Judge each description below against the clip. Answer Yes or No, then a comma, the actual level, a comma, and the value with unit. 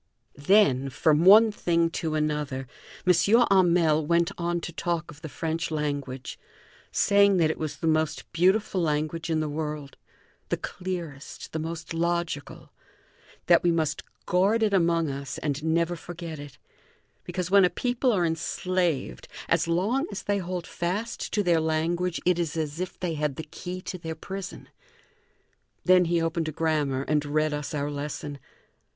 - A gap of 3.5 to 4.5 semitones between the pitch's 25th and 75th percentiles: No, average, 3.0 semitones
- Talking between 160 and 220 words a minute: Yes, average, 165 wpm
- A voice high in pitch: No, medium, 165 Hz